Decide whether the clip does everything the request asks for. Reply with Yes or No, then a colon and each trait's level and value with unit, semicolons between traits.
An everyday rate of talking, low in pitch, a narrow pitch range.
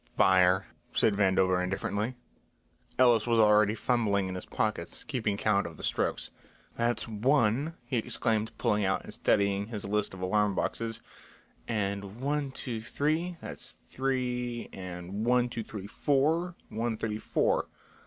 No: average, 145 wpm; low, 110 Hz; average, 3.7 semitones